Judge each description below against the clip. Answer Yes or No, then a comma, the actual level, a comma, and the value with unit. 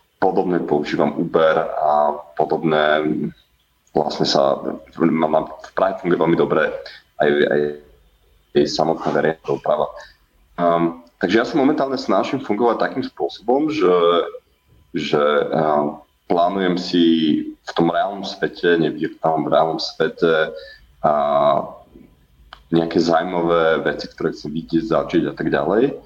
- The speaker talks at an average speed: Yes, average, 125 wpm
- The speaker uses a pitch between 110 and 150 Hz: No, very low, 80 Hz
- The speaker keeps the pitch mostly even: No, average, 3.0 semitones